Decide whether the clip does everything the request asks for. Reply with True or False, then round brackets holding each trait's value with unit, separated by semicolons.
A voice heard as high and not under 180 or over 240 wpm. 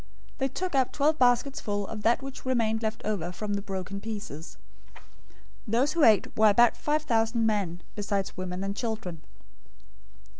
False (220 Hz; 165 wpm)